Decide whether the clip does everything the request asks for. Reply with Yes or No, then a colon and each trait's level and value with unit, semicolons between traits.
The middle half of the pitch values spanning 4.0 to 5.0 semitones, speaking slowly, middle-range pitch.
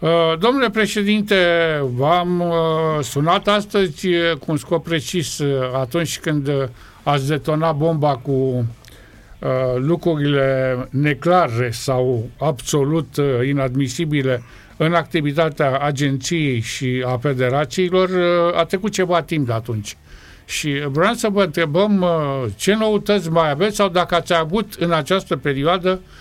Yes: average, 4.7 semitones; slow, 110 wpm; medium, 155 Hz